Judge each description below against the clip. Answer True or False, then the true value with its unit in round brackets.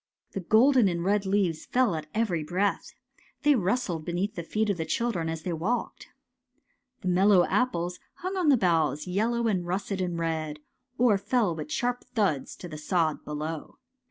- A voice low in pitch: False (185 Hz)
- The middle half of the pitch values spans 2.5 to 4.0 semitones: False (5.1 semitones)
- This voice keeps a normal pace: True (180 wpm)